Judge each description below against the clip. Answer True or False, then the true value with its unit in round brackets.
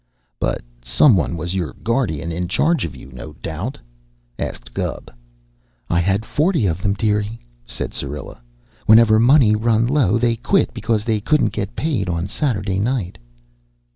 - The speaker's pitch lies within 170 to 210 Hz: False (105 Hz)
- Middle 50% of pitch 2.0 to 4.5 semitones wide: False (5.0 semitones)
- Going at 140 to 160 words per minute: True (155 wpm)